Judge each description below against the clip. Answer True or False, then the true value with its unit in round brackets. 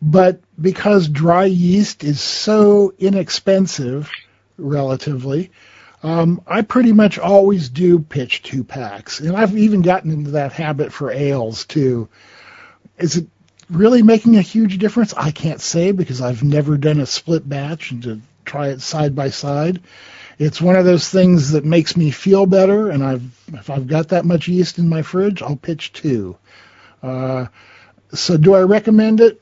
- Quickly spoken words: False (165 wpm)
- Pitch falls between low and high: True (165 Hz)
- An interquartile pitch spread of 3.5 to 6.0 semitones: True (5.1 semitones)